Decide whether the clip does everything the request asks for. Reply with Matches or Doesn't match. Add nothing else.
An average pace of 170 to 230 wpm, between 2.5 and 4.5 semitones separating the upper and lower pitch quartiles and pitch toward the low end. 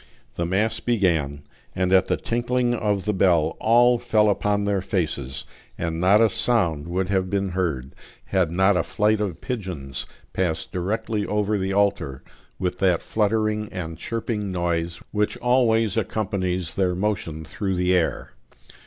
Doesn't match